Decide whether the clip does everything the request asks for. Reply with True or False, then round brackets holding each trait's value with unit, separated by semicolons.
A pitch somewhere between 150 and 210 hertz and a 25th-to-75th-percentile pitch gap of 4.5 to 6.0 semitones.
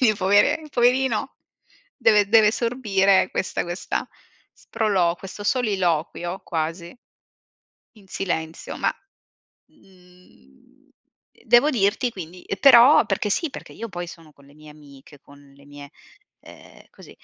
True (190 Hz; 5.6 semitones)